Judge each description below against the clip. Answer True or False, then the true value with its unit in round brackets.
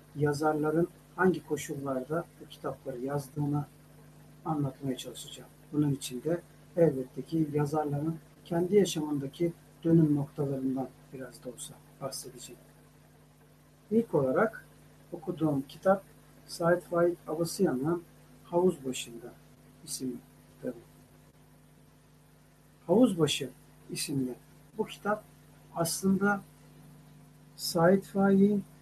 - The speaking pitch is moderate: True (150 Hz)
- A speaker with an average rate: False (85 wpm)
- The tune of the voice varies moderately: True (3.7 semitones)